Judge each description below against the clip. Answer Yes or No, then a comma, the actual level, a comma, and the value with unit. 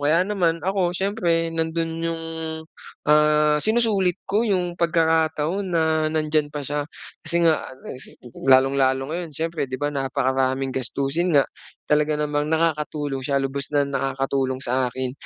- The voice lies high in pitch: No, medium, 150 Hz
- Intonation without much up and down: No, average, 3.5 semitones